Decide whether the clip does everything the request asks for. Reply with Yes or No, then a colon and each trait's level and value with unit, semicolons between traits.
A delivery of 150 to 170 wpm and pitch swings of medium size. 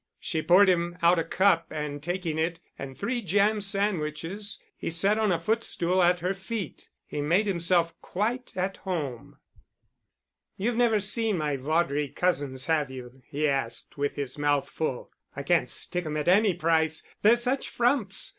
Yes: average, 165 wpm; average, 5.0 semitones